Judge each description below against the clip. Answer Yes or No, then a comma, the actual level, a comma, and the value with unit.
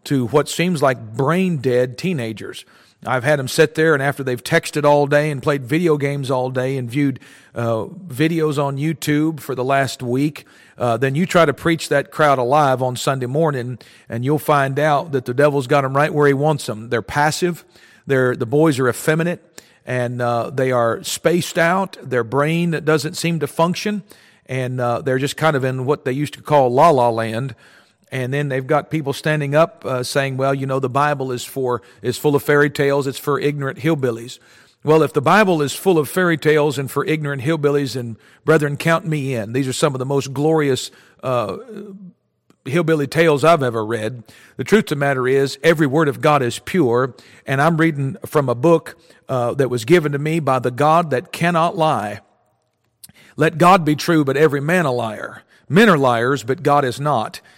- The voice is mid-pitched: Yes, medium, 145 Hz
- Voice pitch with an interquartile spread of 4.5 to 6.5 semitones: No, average, 3.4 semitones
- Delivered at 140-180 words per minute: No, fast, 205 wpm